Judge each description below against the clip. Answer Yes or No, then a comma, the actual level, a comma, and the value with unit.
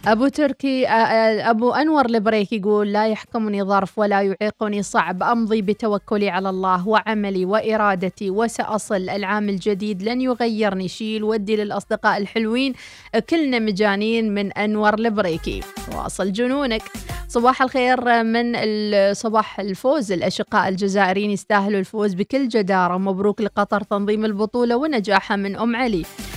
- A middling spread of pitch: No, narrow, 2.3 semitones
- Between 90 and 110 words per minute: No, average, 120 wpm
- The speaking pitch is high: Yes, high, 215 Hz